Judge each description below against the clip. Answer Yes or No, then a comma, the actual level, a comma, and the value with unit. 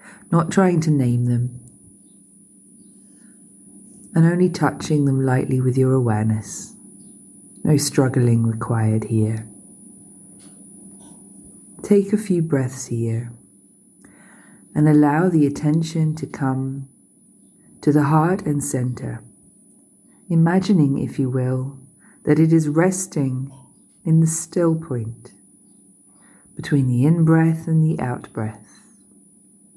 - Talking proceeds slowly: Yes, slow, 105 wpm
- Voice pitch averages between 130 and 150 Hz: Yes, medium, 140 Hz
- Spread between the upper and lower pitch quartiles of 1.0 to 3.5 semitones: No, average, 5.1 semitones